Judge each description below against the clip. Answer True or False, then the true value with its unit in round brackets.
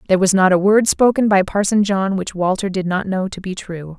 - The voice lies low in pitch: False (190 Hz)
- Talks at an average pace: False (255 wpm)